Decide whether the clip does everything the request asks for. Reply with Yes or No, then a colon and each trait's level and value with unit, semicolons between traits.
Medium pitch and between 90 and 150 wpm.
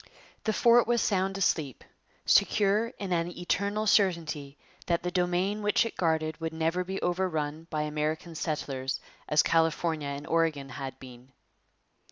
Yes: medium, 165 Hz; average, 145 wpm